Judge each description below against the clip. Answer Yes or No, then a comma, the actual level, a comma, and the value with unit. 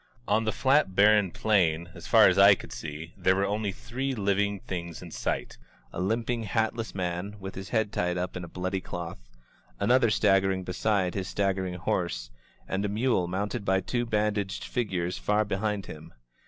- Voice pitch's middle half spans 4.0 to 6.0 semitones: No, average, 2.9 semitones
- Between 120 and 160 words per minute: No, average, 180 wpm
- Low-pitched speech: Yes, low, 100 Hz